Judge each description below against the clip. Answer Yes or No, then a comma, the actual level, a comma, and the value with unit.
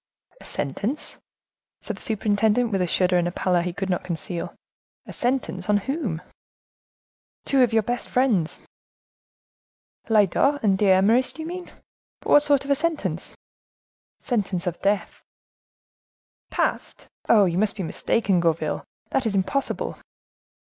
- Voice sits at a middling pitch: No, high, 205 Hz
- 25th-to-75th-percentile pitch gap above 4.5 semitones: Yes, wide, 5.6 semitones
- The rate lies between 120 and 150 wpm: Yes, average, 140 wpm